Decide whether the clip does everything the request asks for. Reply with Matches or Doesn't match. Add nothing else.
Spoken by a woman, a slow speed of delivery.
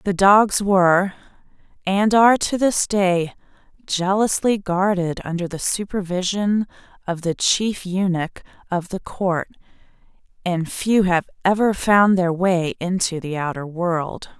Matches